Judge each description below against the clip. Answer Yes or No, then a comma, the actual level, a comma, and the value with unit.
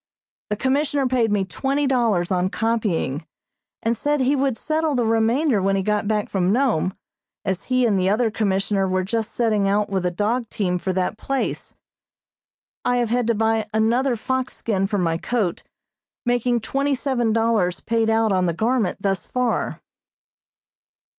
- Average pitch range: Yes, average, 4.1 semitones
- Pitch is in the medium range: No, high, 225 Hz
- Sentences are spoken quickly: No, average, 170 wpm